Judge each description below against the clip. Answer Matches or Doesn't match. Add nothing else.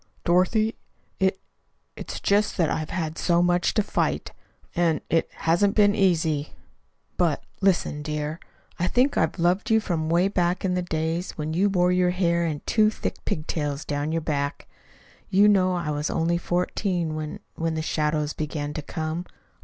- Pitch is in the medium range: Matches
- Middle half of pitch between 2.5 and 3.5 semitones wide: Matches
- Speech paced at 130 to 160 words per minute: Doesn't match